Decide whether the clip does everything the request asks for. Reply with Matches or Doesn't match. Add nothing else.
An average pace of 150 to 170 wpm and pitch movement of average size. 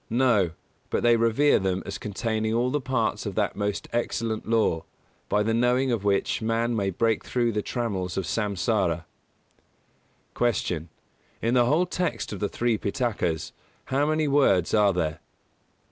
Matches